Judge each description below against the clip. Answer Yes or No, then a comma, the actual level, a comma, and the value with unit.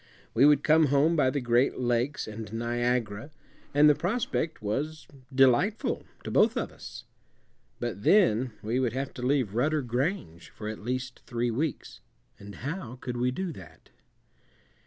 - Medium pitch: No, low, 125 Hz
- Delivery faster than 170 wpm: No, average, 155 wpm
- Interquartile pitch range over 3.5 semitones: Yes, average, 4.0 semitones